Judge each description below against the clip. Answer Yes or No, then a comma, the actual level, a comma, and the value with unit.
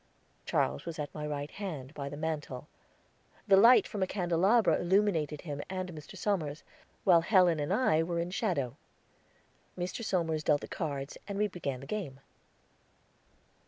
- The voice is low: No, medium, 165 Hz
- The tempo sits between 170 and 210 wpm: No, average, 160 wpm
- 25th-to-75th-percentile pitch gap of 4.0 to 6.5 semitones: Yes, average, 4.4 semitones